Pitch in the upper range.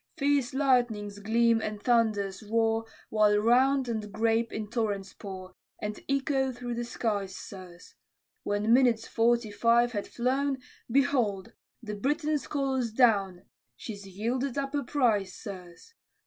Yes: high, 230 Hz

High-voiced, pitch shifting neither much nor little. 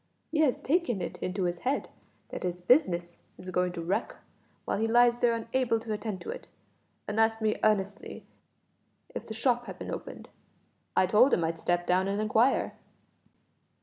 Yes: high, 215 Hz; average, 4.9 semitones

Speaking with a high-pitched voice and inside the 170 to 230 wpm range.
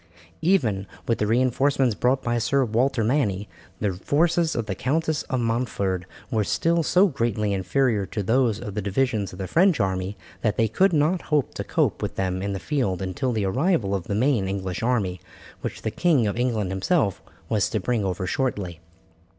No: low, 115 Hz; average, 190 wpm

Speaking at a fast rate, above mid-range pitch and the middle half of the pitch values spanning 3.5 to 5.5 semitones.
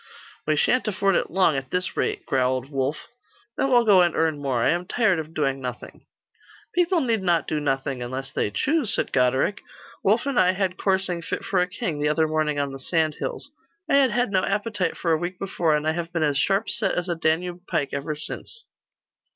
No: fast, 215 wpm; medium, 170 Hz; average, 5.1 semitones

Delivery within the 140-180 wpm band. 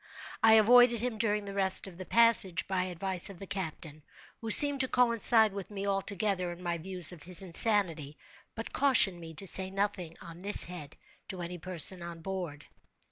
No: average, 190 wpm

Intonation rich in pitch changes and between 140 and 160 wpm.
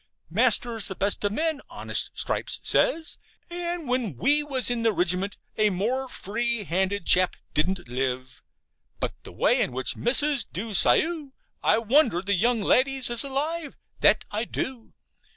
Yes: wide, 6.1 semitones; average, 155 wpm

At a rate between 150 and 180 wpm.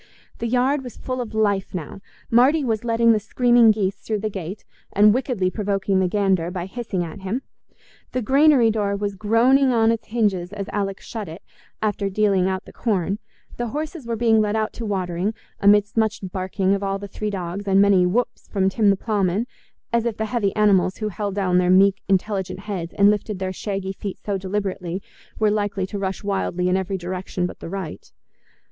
No: average, 200 wpm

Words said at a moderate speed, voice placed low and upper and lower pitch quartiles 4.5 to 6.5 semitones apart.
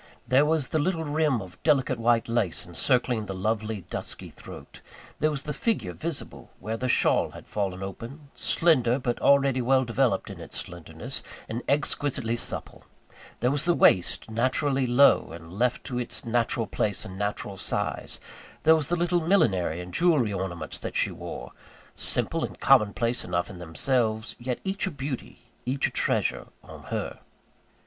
Yes: average, 170 wpm; low, 120 Hz; wide, 5.5 semitones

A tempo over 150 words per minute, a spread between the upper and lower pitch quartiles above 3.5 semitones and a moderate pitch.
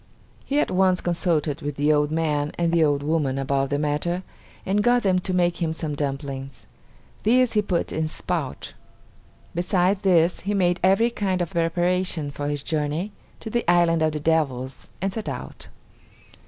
Yes: average, 180 wpm; average, 4.0 semitones; medium, 165 Hz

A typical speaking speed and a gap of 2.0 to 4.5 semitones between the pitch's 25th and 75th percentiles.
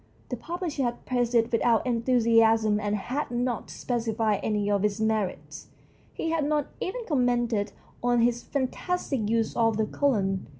Yes: average, 160 wpm; average, 2.8 semitones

